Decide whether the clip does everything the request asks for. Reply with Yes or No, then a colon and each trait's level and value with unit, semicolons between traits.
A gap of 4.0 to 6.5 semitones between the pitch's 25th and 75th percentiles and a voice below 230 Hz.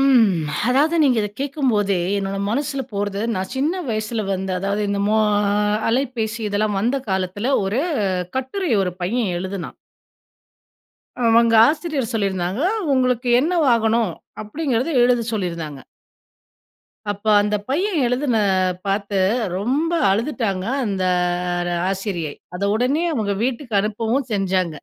Yes: average, 4.9 semitones; high, 220 Hz